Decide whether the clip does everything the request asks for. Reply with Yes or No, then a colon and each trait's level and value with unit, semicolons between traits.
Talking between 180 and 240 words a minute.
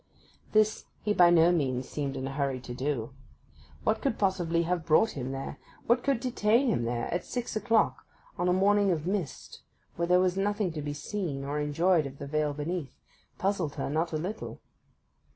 Yes: average, 190 wpm